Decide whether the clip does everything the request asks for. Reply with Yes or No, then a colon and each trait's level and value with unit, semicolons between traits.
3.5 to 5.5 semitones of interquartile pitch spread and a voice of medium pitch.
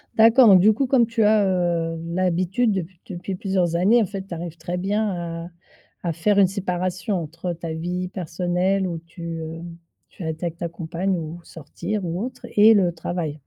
No: average, 2.8 semitones; medium, 180 Hz